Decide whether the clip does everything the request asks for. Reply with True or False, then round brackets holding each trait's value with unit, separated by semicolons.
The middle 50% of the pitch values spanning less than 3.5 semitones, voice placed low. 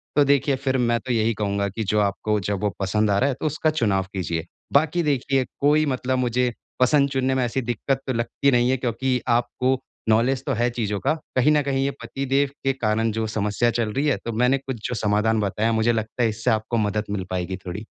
False (3.9 semitones; 120 Hz)